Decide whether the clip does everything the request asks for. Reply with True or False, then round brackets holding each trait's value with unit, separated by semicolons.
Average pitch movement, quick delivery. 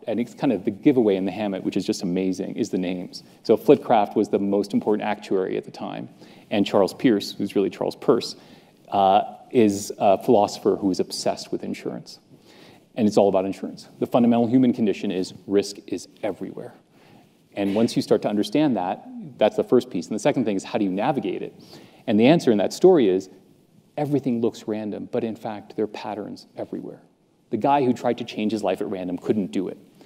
True (4.1 semitones; 210 wpm)